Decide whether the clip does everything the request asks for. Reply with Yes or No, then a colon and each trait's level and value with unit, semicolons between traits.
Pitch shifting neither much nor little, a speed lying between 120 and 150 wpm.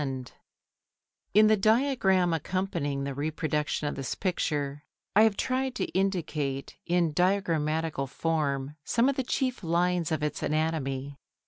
Yes: average, 5.0 semitones; average, 140 wpm